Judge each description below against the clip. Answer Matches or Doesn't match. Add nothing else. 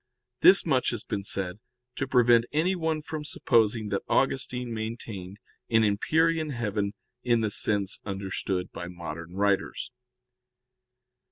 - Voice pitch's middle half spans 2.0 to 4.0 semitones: Doesn't match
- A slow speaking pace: Matches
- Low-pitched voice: Matches